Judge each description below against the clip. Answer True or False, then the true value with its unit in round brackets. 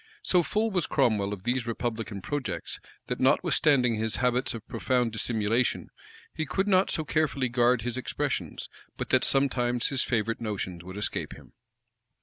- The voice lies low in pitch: True (120 Hz)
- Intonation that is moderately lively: True (3.7 semitones)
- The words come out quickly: False (160 wpm)